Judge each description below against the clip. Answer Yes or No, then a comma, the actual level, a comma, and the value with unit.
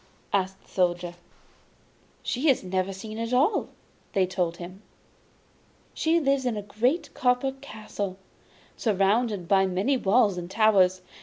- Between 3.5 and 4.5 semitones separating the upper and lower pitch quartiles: No, average, 5.0 semitones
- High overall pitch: Yes, high, 205 Hz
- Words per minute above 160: No, average, 145 wpm